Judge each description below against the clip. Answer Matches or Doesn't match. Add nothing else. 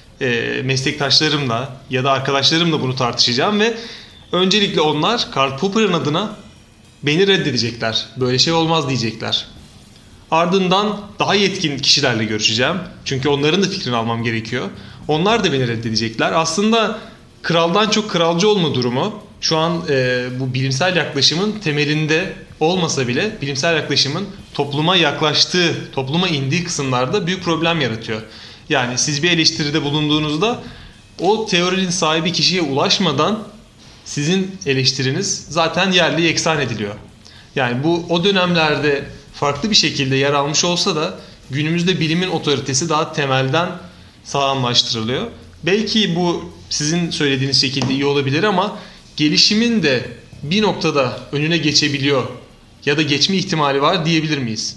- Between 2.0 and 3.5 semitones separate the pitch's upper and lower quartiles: Doesn't match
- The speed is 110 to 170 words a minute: Matches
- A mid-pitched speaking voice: Matches